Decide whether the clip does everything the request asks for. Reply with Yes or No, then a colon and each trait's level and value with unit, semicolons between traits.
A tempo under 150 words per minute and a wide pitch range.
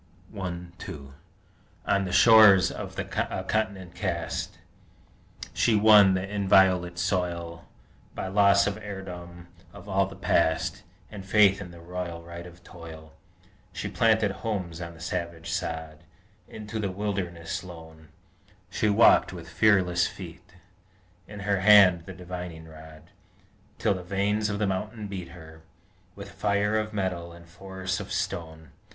No: average, 140 wpm; average, 3.0 semitones